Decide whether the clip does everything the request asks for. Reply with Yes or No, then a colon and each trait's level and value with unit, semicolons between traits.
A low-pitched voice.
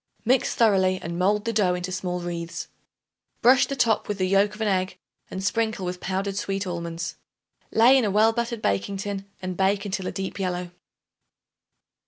No: high, 195 Hz